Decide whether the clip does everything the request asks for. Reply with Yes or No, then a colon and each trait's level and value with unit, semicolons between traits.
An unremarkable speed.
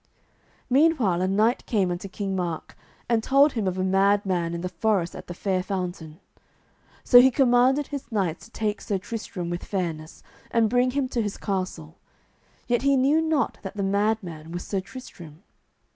Yes: average, 185 wpm